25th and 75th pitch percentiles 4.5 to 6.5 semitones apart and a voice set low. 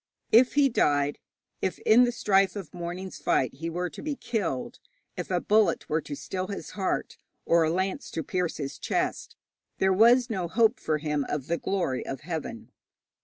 No: average, 5.2 semitones; medium, 180 Hz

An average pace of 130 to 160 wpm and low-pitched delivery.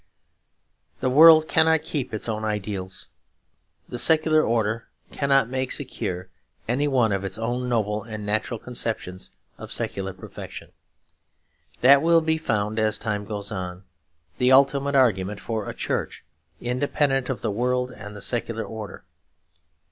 Yes: average, 140 wpm; low, 115 Hz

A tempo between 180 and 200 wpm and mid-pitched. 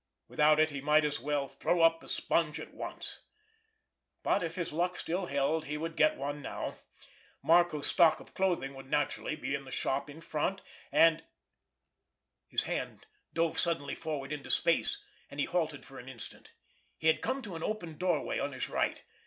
Yes: average, 185 wpm; medium, 155 Hz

